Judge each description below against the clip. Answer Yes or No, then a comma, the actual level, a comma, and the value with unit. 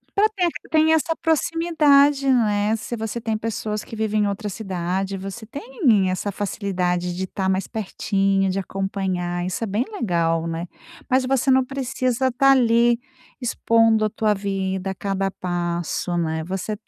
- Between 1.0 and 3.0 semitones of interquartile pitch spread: No, average, 4.6 semitones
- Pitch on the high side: Yes, high, 210 Hz